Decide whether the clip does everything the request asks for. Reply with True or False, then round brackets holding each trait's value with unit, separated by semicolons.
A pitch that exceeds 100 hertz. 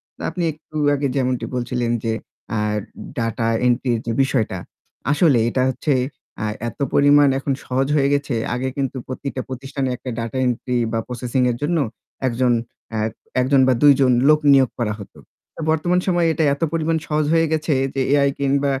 True (135 Hz)